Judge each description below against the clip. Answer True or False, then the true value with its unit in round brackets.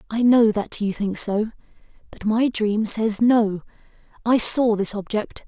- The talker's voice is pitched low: False (220 Hz)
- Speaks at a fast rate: False (155 wpm)